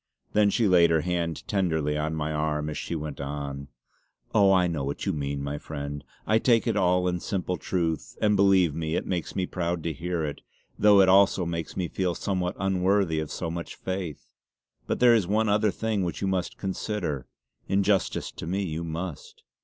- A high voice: No, very low, 90 Hz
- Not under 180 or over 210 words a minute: Yes, average, 200 wpm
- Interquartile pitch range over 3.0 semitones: Yes, average, 3.7 semitones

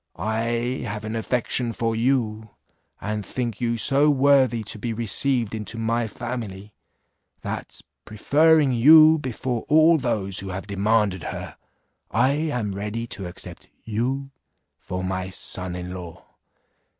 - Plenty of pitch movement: No, average, 3.8 semitones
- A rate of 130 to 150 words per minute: Yes, slow, 135 wpm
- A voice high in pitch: No, low, 115 Hz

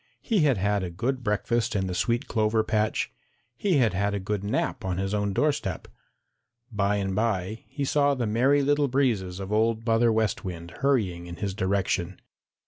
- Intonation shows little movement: No, average, 4.0 semitones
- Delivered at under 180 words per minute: No, average, 185 wpm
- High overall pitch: No, low, 105 Hz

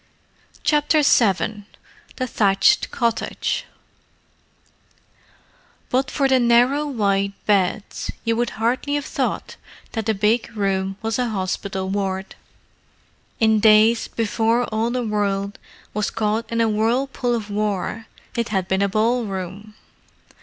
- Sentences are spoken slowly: Yes, slow, 125 wpm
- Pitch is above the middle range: Yes, high, 220 Hz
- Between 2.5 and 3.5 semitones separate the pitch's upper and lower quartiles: Yes, average, 3.0 semitones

